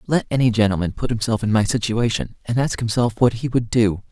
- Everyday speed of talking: No, fast, 220 wpm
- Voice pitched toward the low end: Yes, low, 110 Hz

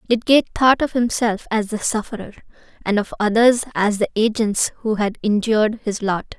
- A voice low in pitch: No, high, 220 Hz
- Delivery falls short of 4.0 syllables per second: No, 5.2 syllables/s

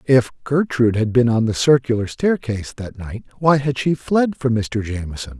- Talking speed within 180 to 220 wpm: Yes, average, 190 wpm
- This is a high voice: No, low, 125 Hz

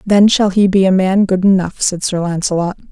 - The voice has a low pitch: No, high, 190 Hz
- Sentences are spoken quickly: Yes, fast, 225 wpm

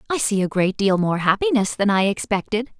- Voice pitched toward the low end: No, high, 210 Hz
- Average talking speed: No, fast, 215 wpm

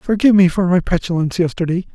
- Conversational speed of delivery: Yes, average, 185 wpm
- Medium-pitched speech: Yes, medium, 180 Hz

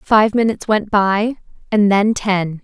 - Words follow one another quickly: No, average, 160 wpm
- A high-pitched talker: Yes, high, 205 Hz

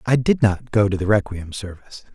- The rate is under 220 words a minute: No, fast, 225 wpm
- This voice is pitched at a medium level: No, low, 105 Hz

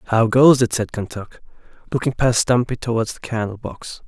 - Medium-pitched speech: No, low, 120 Hz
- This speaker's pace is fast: No, average, 175 wpm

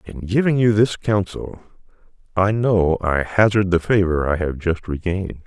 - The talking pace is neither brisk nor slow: Yes, average, 165 wpm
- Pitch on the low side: Yes, very low, 95 Hz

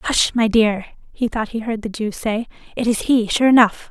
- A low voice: No, high, 225 Hz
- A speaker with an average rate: No, fast, 230 wpm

